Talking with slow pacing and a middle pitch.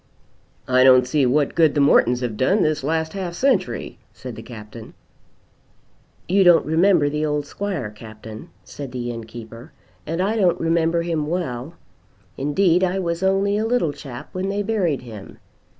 No: average, 165 wpm; medium, 155 Hz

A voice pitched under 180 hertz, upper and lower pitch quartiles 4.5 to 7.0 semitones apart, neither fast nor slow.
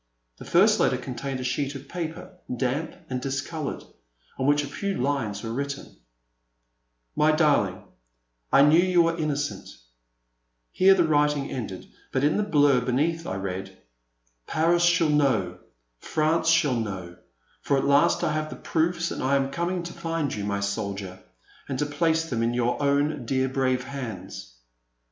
Yes: medium, 140 Hz; average, 5.2 semitones; average, 165 wpm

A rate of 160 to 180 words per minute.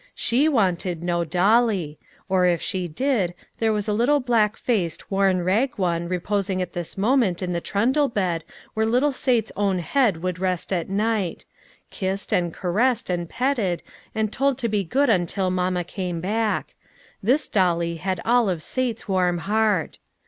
Yes: average, 165 wpm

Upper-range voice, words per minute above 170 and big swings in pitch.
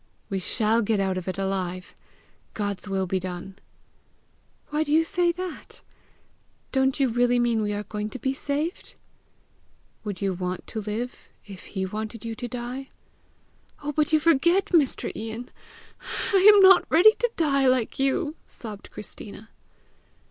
No: high, 235 Hz; average, 155 wpm; wide, 6.5 semitones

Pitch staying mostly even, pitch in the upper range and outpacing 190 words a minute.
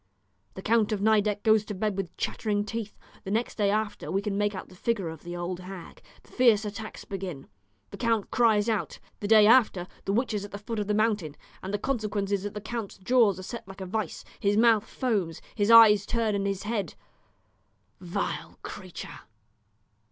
Yes: narrow, 2.2 semitones; high, 205 Hz; fast, 205 wpm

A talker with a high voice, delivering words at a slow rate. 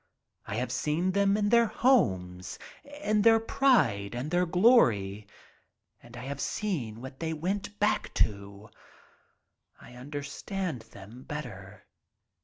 No: medium, 145 Hz; slow, 125 wpm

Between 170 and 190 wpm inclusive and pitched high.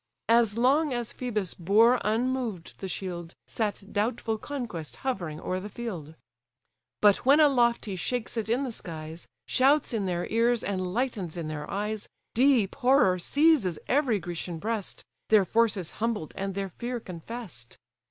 No: average, 155 wpm; high, 215 Hz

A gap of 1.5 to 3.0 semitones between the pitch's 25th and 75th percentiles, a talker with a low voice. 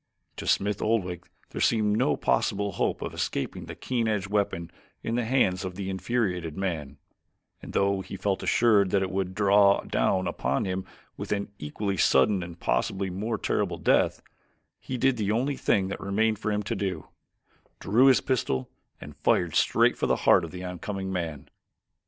Yes: average, 2.7 semitones; low, 100 Hz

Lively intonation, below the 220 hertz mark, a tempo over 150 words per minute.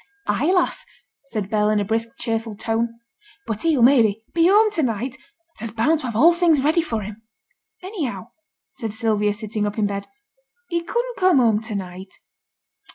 No: wide, 6.9 semitones; high, 230 Hz; average, 180 wpm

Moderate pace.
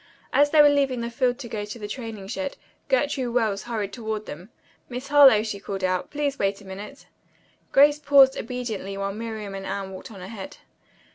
Yes: average, 190 wpm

